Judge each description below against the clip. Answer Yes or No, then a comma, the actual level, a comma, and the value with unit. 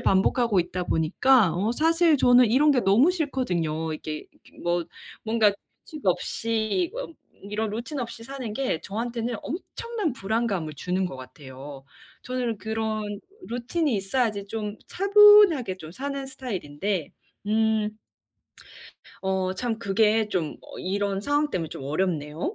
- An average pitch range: No, wide, 5.7 semitones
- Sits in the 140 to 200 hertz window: No, high, 220 Hz